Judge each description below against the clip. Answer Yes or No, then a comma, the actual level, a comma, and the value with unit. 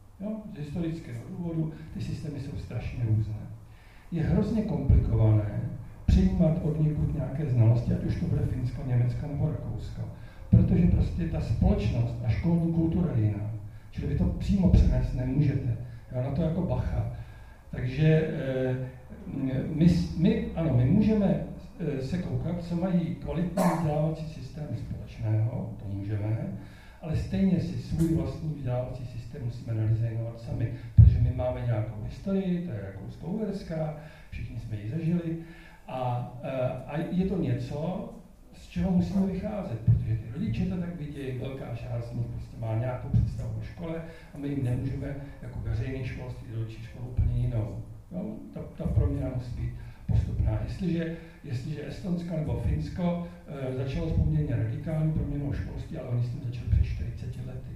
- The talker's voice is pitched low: Yes, low, 130 Hz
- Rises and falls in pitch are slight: No, wide, 5.9 semitones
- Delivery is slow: No, average, 150 wpm